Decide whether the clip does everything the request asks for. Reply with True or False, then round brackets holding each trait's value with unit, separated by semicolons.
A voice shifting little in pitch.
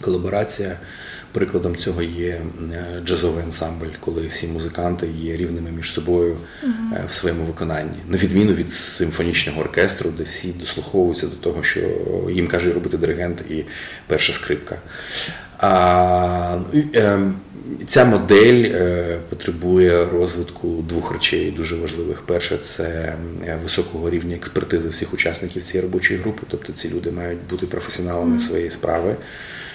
True (1.3 semitones)